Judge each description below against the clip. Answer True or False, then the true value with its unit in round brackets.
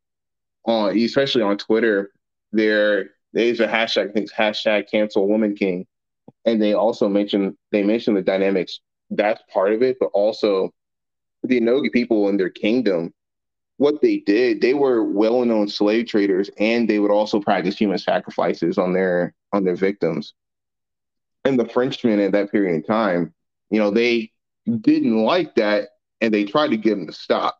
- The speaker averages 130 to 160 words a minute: False (170 wpm)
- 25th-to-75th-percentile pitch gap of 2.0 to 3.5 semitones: True (2.7 semitones)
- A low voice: True (105 Hz)